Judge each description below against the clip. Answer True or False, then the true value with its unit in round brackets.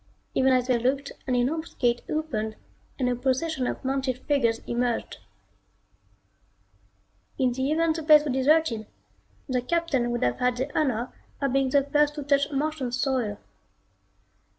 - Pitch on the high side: True (265 Hz)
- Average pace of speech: True (150 wpm)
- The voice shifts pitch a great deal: False (3.1 semitones)